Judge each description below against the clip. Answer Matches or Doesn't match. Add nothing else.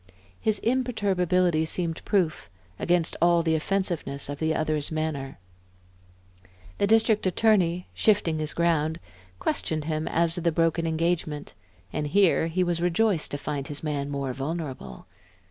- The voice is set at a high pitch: Doesn't match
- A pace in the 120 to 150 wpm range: Matches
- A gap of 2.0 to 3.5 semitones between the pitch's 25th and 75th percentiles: Matches